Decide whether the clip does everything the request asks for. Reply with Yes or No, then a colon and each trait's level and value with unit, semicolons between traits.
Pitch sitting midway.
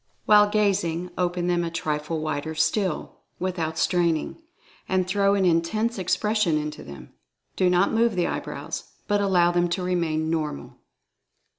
Yes: medium, 175 Hz